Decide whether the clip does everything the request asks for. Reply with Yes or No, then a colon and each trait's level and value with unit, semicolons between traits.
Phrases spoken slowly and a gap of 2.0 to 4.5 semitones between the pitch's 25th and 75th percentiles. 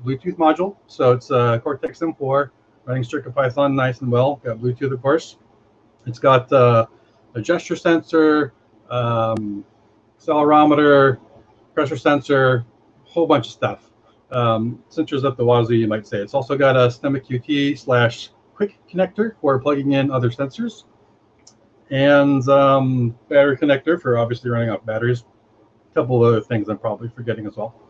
No: average, 160 wpm; average, 4.0 semitones